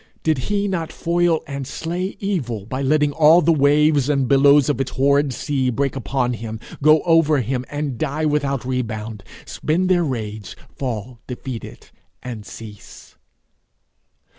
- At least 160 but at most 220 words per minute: No, average, 145 wpm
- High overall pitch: No, medium, 140 Hz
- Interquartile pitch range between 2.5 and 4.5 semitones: Yes, average, 3.8 semitones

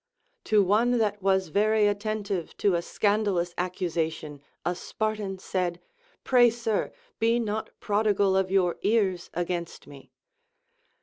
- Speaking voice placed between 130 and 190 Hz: No, high, 200 Hz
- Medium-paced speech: No, slow, 130 wpm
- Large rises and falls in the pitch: No, average, 3.3 semitones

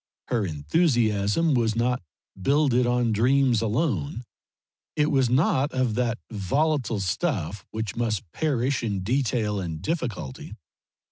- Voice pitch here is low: Yes, low, 120 Hz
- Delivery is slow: Yes, slow, 120 wpm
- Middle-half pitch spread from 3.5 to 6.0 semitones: Yes, average, 4.5 semitones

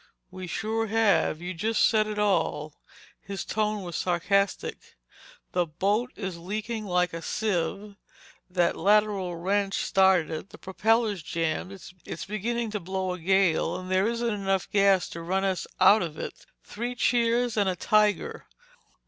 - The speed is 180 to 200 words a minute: No, average, 155 wpm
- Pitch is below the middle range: No, high, 195 Hz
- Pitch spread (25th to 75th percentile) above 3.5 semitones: No, average, 3.0 semitones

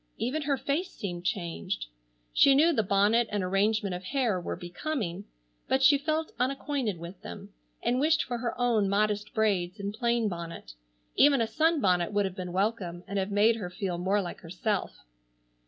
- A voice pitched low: No, high, 205 Hz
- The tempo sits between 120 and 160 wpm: No, average, 175 wpm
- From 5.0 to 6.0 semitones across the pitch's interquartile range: Yes, wide, 5.4 semitones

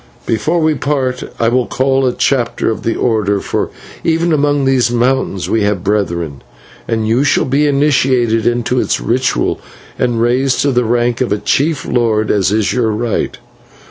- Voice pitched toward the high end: No, low, 120 Hz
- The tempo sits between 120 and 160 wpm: No, average, 175 wpm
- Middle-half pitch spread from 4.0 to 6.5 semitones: No, average, 3.3 semitones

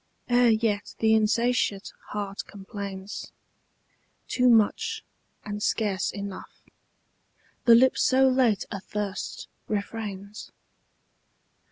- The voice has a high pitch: Yes, high, 210 Hz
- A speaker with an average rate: No, slow, 85 wpm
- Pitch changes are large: No, narrow, 2.6 semitones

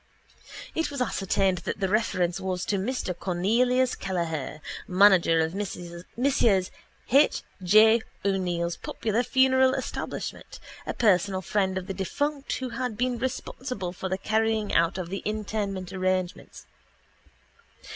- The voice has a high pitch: Yes, high, 195 Hz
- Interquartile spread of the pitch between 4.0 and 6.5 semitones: Yes, average, 4.4 semitones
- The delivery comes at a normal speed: No, slow, 130 wpm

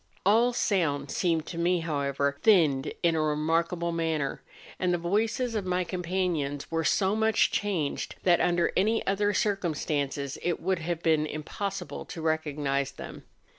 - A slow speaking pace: No, average, 155 wpm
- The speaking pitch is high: No, medium, 170 Hz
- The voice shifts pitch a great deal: No, average, 3.8 semitones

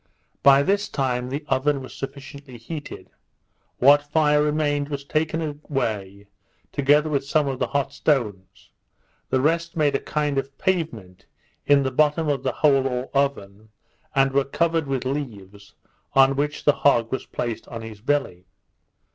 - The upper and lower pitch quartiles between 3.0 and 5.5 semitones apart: No, narrow, 2.6 semitones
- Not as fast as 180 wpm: Yes, average, 155 wpm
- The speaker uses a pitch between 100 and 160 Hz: Yes, medium, 140 Hz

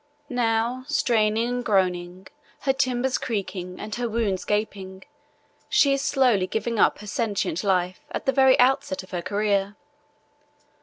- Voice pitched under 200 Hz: No, high, 220 Hz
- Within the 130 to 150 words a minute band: Yes, average, 145 wpm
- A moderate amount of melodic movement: Yes, average, 4.7 semitones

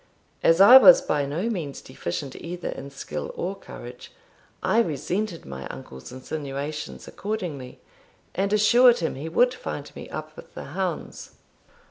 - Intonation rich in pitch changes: Yes, wide, 6.3 semitones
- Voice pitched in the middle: Yes, medium, 160 Hz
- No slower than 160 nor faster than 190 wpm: No, average, 145 wpm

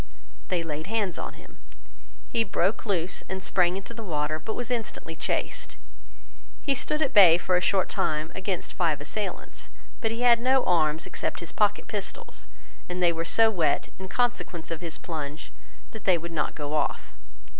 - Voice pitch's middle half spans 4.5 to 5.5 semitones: Yes, average, 5.1 semitones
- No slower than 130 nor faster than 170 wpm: No, average, 180 wpm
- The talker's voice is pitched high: No, medium, 180 Hz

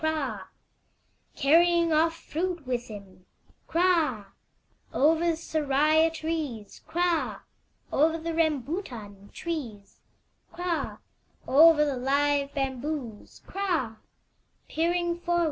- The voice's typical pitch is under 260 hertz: No, very high, 305 Hz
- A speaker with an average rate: No, slow, 80 wpm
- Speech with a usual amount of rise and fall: Yes, average, 4.4 semitones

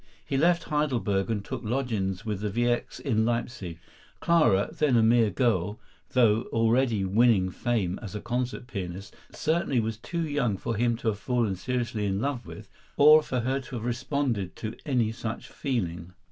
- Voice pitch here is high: No, low, 115 Hz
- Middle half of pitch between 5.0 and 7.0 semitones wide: No, average, 3.7 semitones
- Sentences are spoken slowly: No, average, 175 wpm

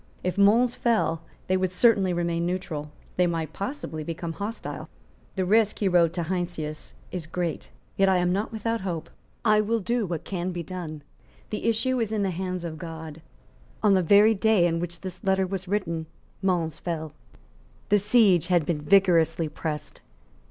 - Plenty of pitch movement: No, average, 3.3 semitones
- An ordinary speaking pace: Yes, average, 175 wpm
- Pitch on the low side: No, medium, 180 Hz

